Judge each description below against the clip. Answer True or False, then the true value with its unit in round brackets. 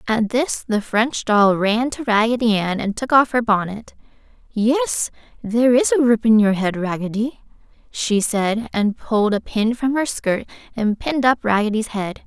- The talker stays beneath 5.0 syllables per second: True (4.5 syllables/s)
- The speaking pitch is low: False (225 Hz)